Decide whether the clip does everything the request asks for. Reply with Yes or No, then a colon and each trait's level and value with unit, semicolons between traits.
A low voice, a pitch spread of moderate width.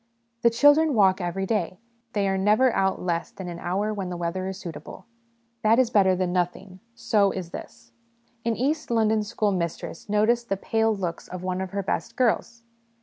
No: high, 195 Hz; average, 3.5 semitones